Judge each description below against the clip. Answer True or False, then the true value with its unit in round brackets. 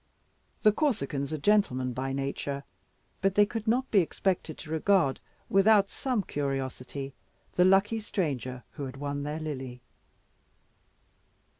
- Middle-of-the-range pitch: True (155 Hz)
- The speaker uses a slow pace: True (130 wpm)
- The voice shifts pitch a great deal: True (6.8 semitones)